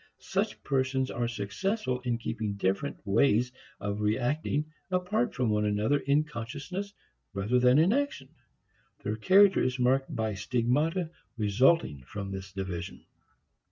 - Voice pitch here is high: No, low, 125 Hz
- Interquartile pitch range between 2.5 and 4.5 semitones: No, wide, 5.5 semitones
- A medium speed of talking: No, slow, 130 wpm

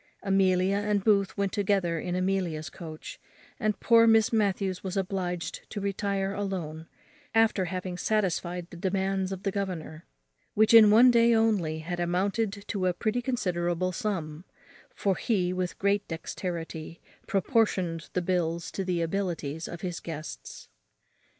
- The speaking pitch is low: No, high, 190 Hz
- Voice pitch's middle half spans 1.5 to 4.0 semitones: Yes, average, 2.8 semitones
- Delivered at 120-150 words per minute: Yes, average, 145 wpm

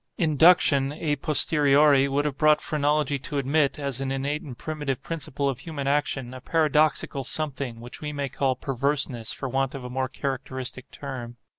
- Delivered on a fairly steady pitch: Yes, narrow, 2.1 semitones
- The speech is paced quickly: No, average, 170 wpm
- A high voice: No, medium, 140 Hz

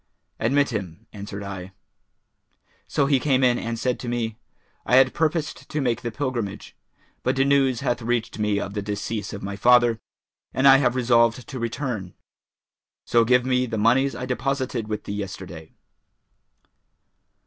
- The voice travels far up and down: No, average, 3.6 semitones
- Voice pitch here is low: Yes, low, 120 Hz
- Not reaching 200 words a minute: Yes, average, 160 wpm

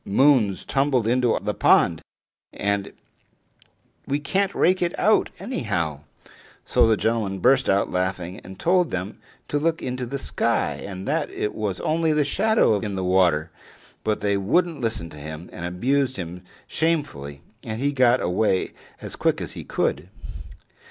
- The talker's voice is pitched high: No, low, 110 Hz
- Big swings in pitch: Yes, wide, 7.3 semitones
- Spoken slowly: No, average, 160 wpm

